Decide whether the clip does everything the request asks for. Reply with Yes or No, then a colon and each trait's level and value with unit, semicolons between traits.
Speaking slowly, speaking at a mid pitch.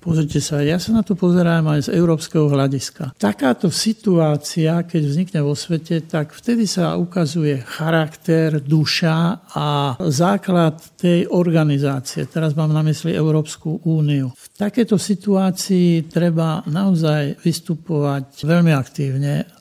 No: average, 125 wpm; medium, 160 Hz